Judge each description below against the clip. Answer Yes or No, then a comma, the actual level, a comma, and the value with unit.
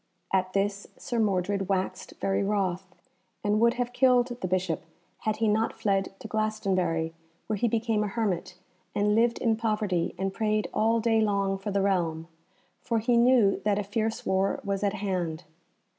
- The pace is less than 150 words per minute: No, average, 175 wpm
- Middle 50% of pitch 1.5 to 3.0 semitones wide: Yes, narrow, 2.6 semitones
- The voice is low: No, high, 205 Hz